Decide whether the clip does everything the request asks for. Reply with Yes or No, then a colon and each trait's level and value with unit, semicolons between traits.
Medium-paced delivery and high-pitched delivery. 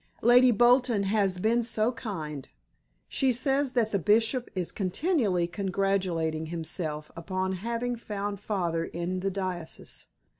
No: slow, 125 wpm; high, 200 Hz